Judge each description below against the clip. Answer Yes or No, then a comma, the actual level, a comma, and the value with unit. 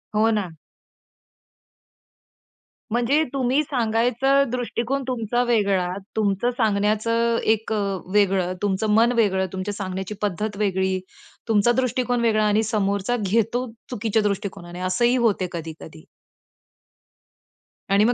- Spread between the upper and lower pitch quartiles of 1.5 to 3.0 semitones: No, average, 3.4 semitones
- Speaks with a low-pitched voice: No, high, 215 Hz